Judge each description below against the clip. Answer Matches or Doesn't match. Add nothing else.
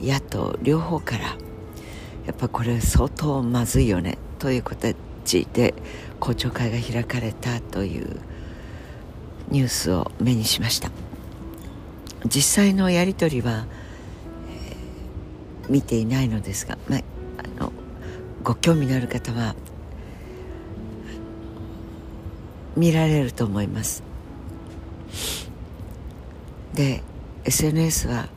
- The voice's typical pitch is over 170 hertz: Doesn't match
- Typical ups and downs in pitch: Doesn't match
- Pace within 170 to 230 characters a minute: Matches